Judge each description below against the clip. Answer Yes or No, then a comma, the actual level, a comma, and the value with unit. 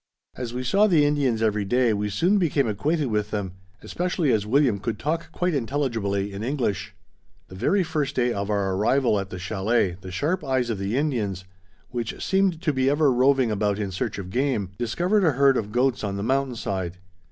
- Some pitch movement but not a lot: No, wide, 6.0 semitones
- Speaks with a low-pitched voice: Yes, low, 120 Hz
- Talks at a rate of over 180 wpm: Yes, average, 200 wpm